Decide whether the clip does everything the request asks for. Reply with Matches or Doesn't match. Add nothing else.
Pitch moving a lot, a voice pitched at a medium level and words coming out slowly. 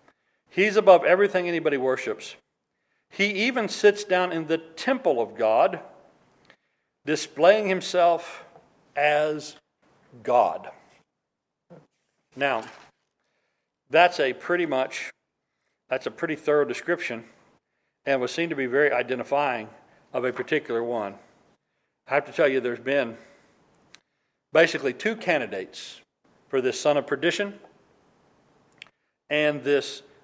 Doesn't match